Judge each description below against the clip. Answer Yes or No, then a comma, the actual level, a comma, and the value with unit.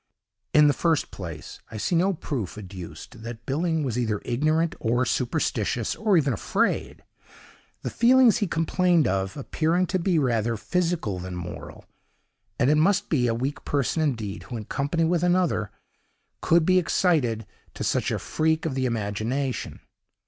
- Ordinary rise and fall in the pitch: No, wide, 6.9 semitones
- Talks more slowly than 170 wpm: Yes, average, 155 wpm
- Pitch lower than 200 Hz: Yes, medium, 140 Hz